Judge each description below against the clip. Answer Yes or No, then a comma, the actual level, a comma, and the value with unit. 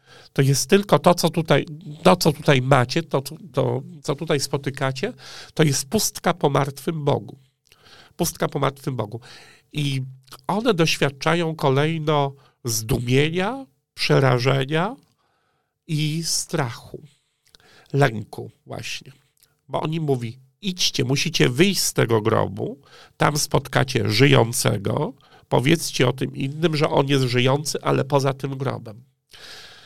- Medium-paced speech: Yes, average, 120 wpm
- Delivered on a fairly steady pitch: No, average, 3.2 semitones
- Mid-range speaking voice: Yes, medium, 145 Hz